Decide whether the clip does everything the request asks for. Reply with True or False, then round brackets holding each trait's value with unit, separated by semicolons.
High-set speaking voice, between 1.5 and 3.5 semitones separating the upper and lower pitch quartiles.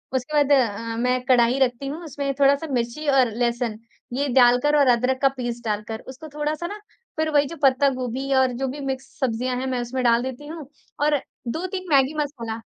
True (260 Hz; 2.9 semitones)